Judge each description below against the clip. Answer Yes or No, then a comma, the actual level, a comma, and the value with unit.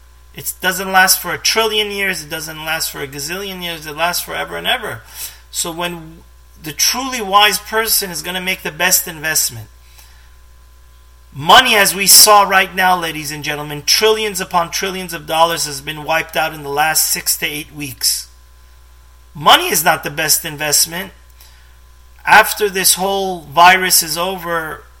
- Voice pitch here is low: No, medium, 160 Hz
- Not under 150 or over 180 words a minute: Yes, average, 165 wpm